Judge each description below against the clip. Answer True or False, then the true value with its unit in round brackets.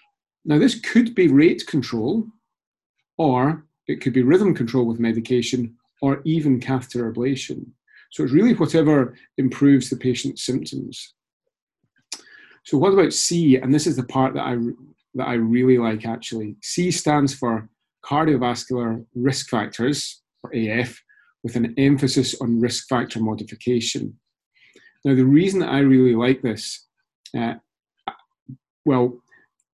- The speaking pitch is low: True (130 Hz)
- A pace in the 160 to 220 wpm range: False (135 wpm)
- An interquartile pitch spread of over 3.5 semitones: False (3.1 semitones)